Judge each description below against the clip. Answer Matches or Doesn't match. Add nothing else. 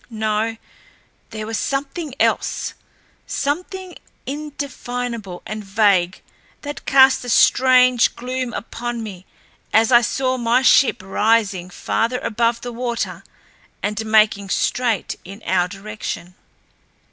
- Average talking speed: Doesn't match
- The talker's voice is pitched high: Matches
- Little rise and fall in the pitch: Doesn't match